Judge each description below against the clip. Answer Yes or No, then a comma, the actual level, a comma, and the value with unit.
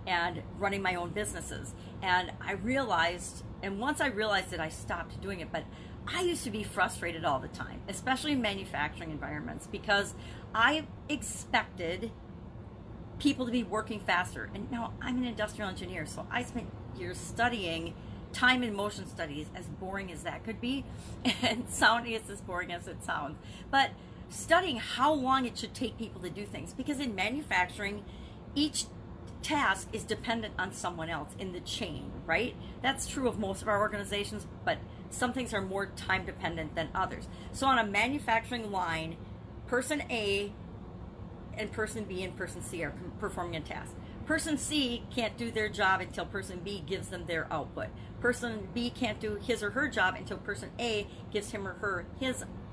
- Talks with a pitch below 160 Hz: No, high, 225 Hz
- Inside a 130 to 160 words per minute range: No, average, 175 wpm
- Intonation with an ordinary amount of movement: Yes, average, 4.2 semitones